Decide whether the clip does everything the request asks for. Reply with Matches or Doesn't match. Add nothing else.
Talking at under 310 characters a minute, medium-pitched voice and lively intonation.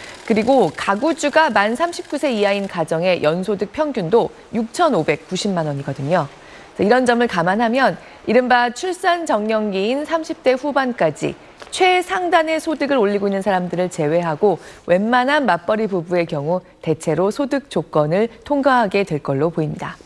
Doesn't match